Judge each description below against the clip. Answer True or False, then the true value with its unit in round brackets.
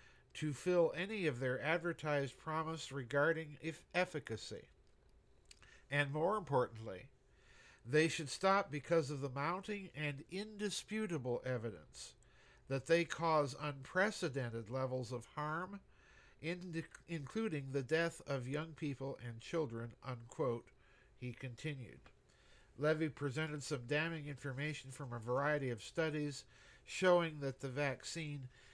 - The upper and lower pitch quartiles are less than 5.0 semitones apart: True (3.9 semitones)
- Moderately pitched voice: True (150 Hz)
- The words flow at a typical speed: False (115 wpm)